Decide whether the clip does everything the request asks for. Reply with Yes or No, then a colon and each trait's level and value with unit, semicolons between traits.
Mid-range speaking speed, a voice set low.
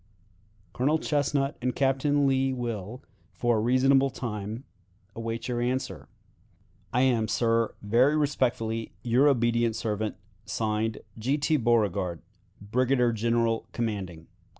No: slow, 115 wpm; low, 120 Hz